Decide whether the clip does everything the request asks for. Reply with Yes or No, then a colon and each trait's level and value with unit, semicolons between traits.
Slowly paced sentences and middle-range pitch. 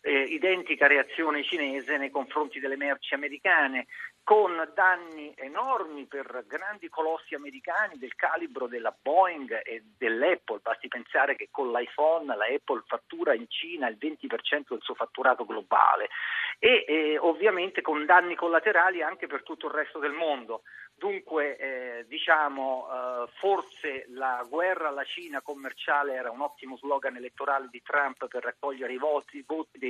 No: average, 150 wpm; medium, 150 Hz